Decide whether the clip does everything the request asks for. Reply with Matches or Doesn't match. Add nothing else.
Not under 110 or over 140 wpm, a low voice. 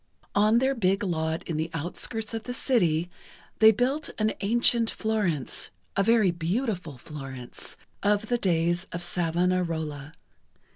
Doesn't match